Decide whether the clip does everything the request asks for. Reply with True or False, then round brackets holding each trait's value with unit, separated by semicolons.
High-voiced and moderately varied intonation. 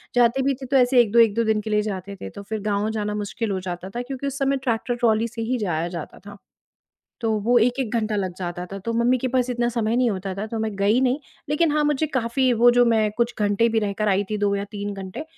True (225 Hz; 3.2 semitones)